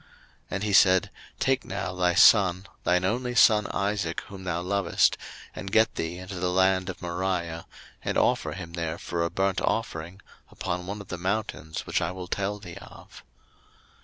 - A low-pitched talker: Yes, very low, 95 Hz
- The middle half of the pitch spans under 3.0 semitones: Yes, narrow, 2.4 semitones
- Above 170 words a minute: Yes, average, 180 wpm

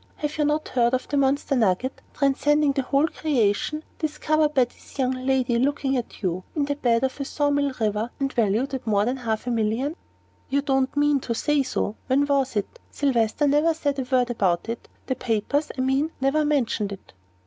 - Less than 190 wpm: No, fast, 205 wpm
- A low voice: No, very high, 265 Hz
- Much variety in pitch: No, average, 3.5 semitones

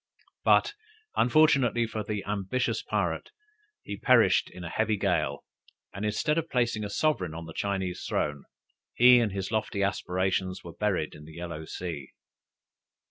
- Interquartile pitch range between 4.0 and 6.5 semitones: Yes, average, 4.4 semitones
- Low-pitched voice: Yes, low, 100 Hz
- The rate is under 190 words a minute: Yes, average, 150 wpm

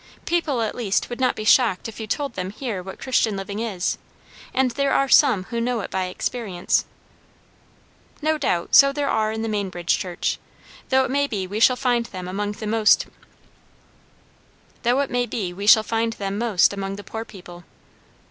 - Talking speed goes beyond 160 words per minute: No, average, 155 wpm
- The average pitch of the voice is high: Yes, high, 220 Hz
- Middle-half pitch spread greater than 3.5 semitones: Yes, average, 4.2 semitones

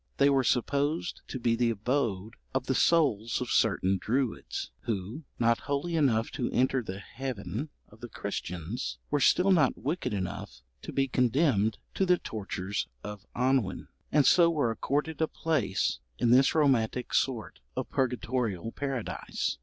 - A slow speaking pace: No, average, 155 wpm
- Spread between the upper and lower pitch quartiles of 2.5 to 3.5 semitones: No, average, 4.7 semitones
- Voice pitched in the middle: No, low, 125 Hz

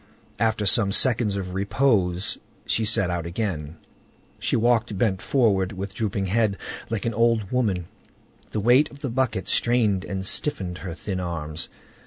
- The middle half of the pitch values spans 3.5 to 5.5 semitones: Yes, average, 3.8 semitones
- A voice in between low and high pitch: No, low, 100 Hz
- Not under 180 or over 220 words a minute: No, average, 155 wpm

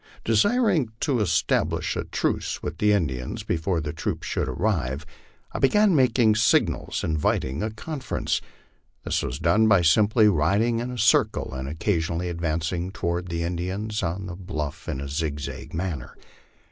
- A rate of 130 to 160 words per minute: Yes, average, 150 wpm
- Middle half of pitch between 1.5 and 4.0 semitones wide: No, wide, 5.5 semitones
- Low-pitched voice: Yes, very low, 90 Hz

